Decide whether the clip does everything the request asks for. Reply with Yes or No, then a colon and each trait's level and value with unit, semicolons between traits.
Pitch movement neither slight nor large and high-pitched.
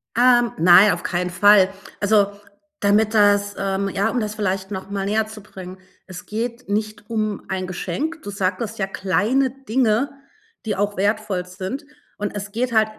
No: narrow, 2.3 semitones; high, 205 Hz